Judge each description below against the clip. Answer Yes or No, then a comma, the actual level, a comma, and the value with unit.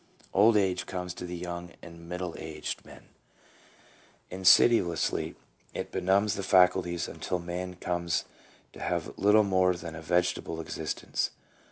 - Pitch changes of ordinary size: No, narrow, 1.4 semitones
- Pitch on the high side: No, very low, 90 Hz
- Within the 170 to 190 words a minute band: No, average, 140 wpm